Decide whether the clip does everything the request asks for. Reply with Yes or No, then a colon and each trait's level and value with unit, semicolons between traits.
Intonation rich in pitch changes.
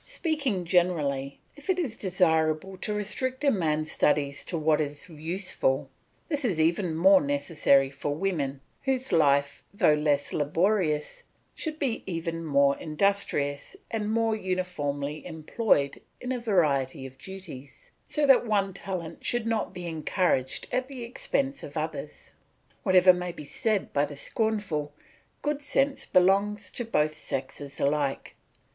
Yes: wide, 6.6 semitones